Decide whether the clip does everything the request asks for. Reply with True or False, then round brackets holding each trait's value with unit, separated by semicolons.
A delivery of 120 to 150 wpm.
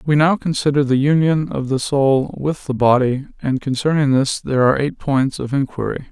False (195 wpm)